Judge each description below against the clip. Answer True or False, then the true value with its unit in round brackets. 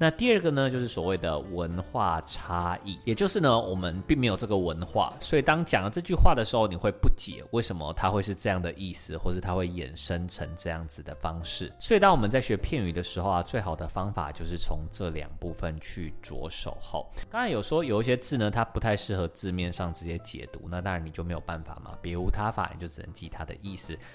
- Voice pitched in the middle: False (90 Hz)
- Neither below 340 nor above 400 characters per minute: True (350 characters per minute)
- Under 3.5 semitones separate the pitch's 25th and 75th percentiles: False (3.8 semitones)